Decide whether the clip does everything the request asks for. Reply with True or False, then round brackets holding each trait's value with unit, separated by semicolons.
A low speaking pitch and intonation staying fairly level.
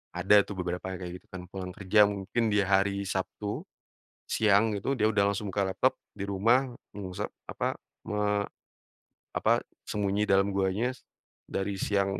True (100 Hz; 1.4 semitones)